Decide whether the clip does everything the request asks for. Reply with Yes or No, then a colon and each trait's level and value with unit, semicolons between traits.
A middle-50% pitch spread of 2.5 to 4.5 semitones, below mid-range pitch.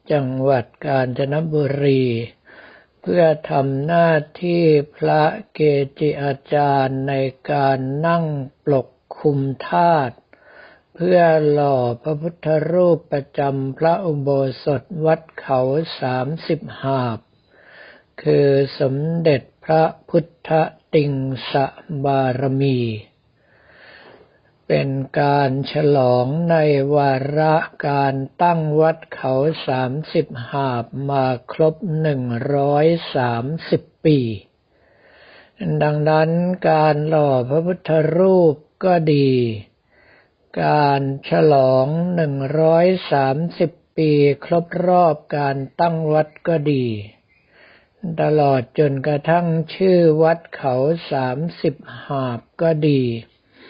No: average, 3.0 semitones; medium, 145 Hz